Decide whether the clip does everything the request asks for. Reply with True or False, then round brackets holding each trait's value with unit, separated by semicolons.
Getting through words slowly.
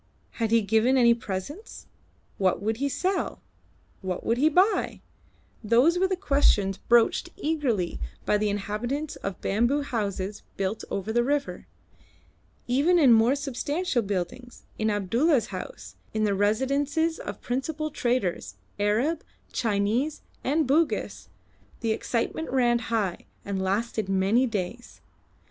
True (130 wpm)